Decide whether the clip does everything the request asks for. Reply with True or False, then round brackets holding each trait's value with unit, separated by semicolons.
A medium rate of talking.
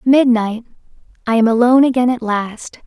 False (125 wpm)